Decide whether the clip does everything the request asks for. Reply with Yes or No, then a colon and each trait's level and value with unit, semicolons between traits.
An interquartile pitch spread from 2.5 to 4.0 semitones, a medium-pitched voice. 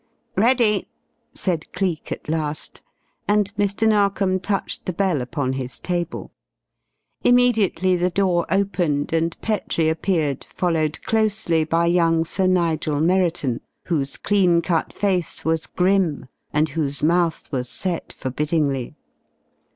Yes: average, 3.6 semitones; medium, 170 Hz